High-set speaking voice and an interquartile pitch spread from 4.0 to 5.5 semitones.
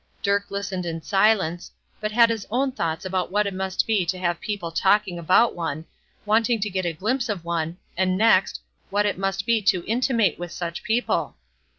No: high, 195 Hz; average, 3.6 semitones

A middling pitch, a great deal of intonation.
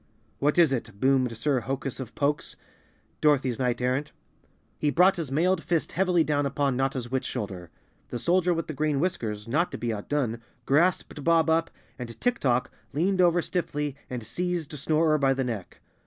No: medium, 145 Hz; average, 4.8 semitones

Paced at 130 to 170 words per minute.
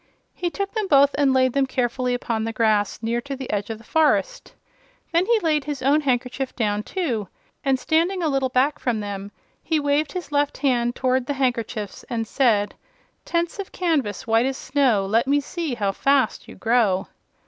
No: average, 190 wpm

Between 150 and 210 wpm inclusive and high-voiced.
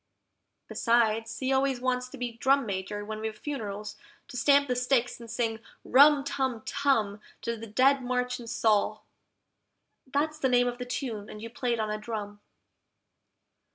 Yes: average, 170 wpm; high, 240 Hz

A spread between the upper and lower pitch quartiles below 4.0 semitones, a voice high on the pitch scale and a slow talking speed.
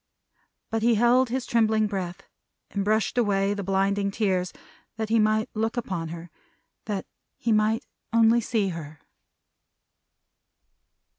Yes: narrow, 2.6 semitones; high, 215 Hz; slow, 130 wpm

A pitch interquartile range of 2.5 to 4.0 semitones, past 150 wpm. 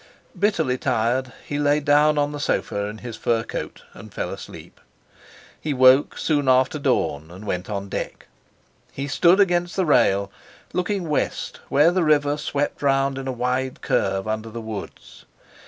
No: average, 4.8 semitones; average, 165 wpm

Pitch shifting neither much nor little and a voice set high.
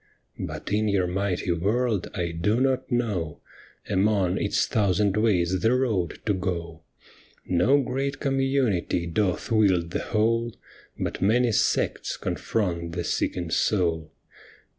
No: average, 4.8 semitones; low, 100 Hz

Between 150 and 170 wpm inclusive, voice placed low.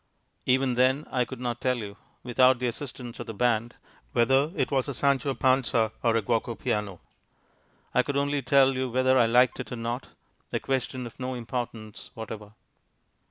No: average, 180 wpm; low, 125 Hz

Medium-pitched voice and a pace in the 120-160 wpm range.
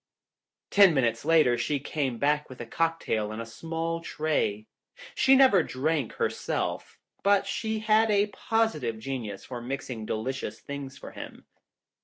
Yes: medium, 145 Hz; average, 150 wpm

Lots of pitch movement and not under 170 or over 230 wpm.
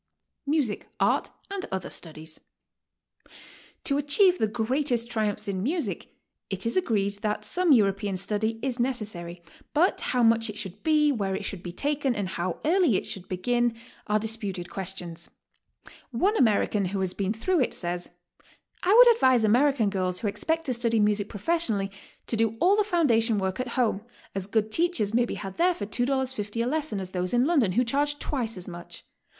Yes: wide, 6.0 semitones; average, 180 wpm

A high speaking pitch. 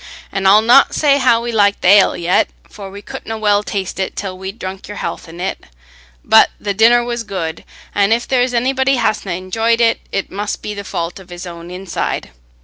Yes: high, 205 Hz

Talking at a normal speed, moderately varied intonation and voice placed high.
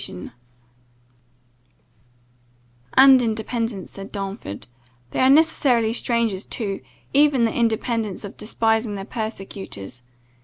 No: slow, 105 wpm; average, 3.5 semitones; high, 225 Hz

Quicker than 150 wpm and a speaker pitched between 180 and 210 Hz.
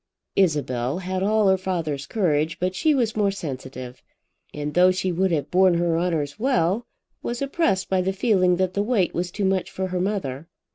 Yes: average, 190 wpm; medium, 185 Hz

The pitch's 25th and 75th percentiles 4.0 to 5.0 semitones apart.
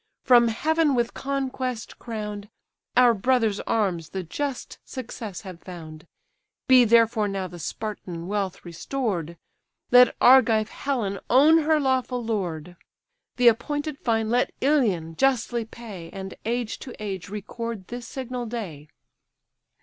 Yes: average, 4.6 semitones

